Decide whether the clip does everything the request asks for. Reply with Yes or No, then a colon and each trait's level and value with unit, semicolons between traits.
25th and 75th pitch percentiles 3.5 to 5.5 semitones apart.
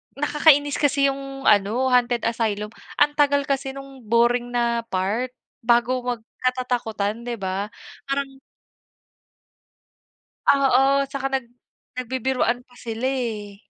No: average, 2.8 semitones